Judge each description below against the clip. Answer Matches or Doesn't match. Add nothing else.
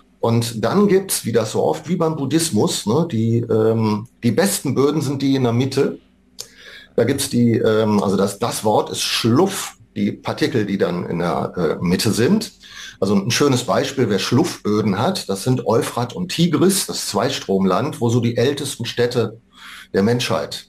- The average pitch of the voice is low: Matches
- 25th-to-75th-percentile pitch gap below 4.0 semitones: Doesn't match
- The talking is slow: Doesn't match